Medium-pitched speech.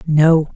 Yes: medium, 155 Hz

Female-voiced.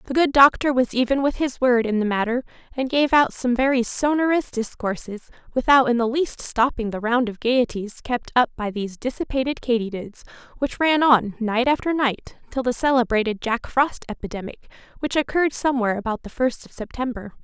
Yes: female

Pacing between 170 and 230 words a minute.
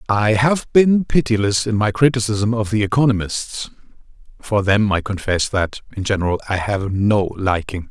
No: average, 160 wpm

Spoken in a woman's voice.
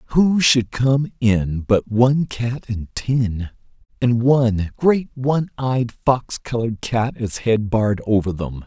No: male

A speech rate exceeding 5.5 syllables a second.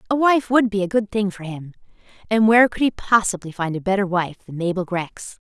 Yes: 5.8 syllables/s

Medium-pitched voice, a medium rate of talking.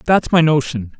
Yes: medium, 150 Hz; average, 180 wpm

